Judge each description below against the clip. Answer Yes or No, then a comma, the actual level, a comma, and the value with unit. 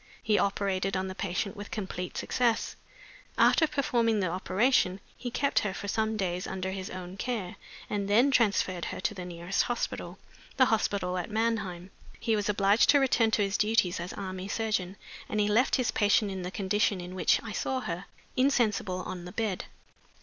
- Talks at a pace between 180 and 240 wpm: Yes, average, 185 wpm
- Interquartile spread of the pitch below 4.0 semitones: Yes, average, 3.1 semitones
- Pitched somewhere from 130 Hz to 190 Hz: No, high, 200 Hz